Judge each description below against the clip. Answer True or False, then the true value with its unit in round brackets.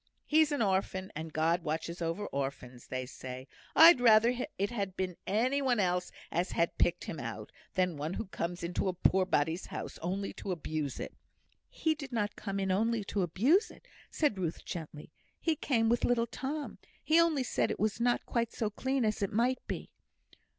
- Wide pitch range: True (6.1 semitones)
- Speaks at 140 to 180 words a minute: False (190 wpm)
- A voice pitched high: True (195 Hz)